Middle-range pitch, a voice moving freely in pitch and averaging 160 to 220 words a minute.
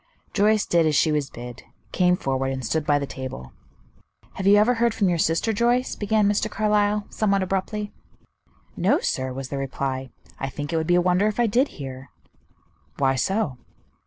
Yes: medium, 180 Hz; wide, 7.6 semitones; average, 190 wpm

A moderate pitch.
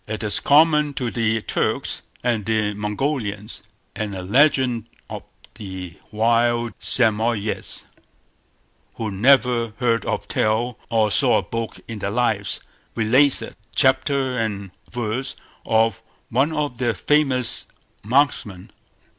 No: low, 115 Hz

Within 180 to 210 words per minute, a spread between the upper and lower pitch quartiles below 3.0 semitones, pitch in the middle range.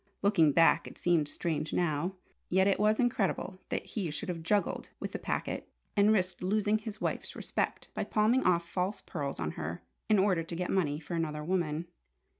No: average, 190 wpm; average, 4.1 semitones; medium, 180 Hz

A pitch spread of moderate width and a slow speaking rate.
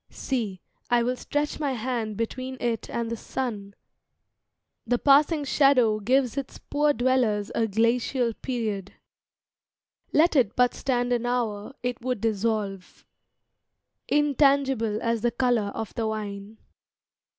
Yes: average, 3.2 semitones; slow, 130 wpm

